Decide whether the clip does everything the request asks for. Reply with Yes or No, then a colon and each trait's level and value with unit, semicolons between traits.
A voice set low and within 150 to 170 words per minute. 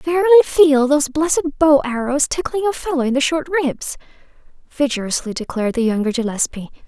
No: very high, 280 Hz; average, 155 wpm